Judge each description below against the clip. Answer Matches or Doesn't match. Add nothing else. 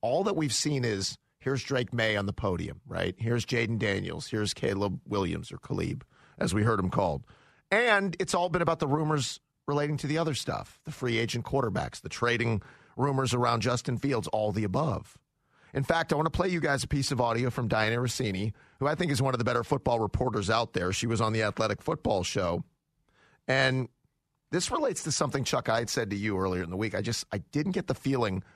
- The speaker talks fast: Matches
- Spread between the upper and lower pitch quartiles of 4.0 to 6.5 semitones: Matches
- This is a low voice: Matches